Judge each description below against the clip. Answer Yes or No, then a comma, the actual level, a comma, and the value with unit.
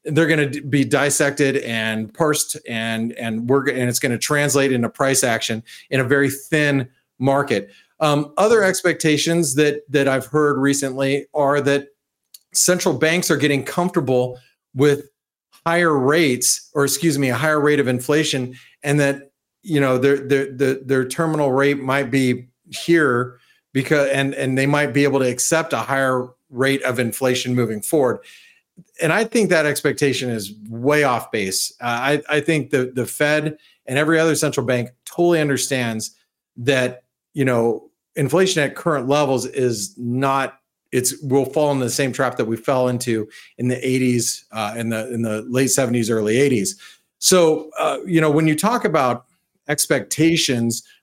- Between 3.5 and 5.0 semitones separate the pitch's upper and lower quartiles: No, average, 3.1 semitones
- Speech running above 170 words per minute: No, average, 165 wpm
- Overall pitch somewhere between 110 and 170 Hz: Yes, medium, 140 Hz